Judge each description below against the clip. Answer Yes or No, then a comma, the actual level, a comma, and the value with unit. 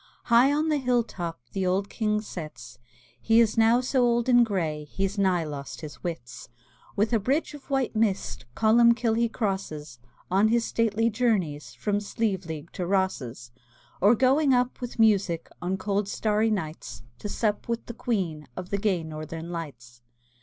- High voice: Yes, high, 205 Hz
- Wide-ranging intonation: Yes, wide, 5.8 semitones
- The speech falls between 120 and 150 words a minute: No, average, 165 wpm